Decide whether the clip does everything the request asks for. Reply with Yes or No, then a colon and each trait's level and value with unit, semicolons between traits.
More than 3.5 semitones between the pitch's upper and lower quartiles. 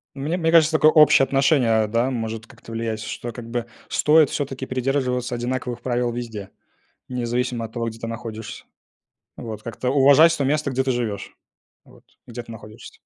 No: average, 2.9 semitones